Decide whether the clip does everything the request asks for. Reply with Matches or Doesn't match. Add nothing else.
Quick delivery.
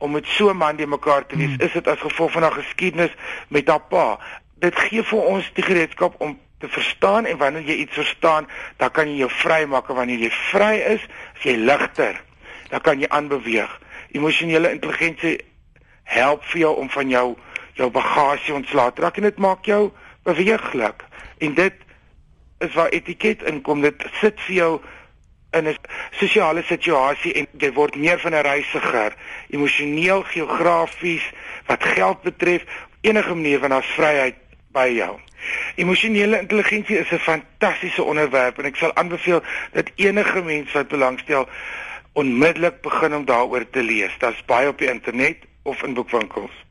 Doesn't match